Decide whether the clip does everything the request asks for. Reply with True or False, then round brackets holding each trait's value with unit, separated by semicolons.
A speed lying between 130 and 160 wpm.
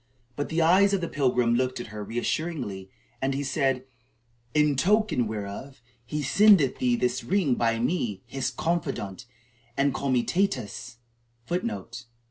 True (145 wpm)